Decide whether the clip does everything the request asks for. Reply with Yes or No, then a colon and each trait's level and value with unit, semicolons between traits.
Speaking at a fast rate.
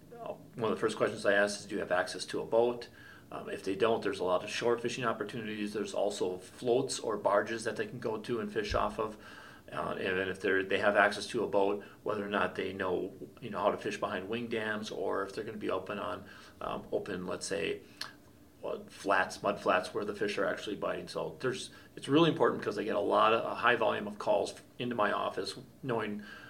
Yes: fast, 240 wpm